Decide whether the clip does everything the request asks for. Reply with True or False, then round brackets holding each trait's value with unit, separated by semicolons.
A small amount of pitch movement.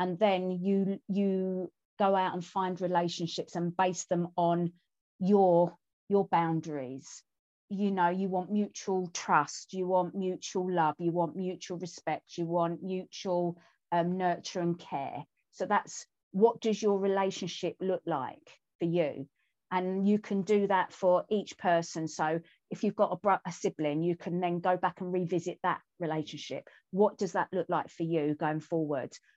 True (2.1 semitones)